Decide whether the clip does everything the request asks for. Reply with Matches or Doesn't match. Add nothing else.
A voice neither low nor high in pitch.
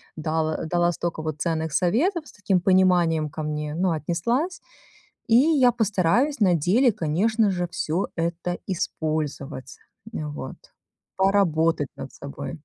Matches